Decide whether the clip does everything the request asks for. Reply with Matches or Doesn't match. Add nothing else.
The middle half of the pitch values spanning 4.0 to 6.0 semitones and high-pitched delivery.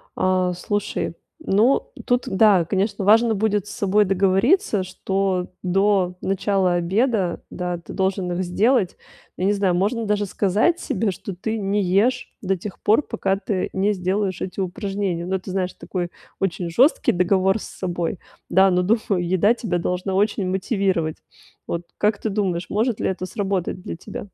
Doesn't match